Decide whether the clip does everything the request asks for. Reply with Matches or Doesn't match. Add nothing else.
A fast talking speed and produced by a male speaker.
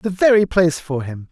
Matches